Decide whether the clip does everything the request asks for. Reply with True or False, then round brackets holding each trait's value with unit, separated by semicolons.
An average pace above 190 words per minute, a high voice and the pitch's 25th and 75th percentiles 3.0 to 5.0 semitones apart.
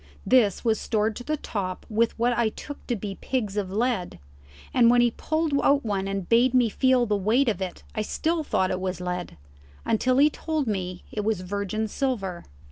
True (205 wpm; 220 Hz; 4.5 semitones)